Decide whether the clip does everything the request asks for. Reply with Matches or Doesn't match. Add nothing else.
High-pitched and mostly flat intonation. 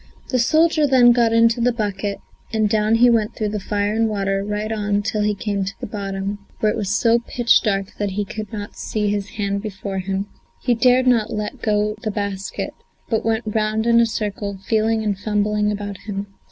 Matches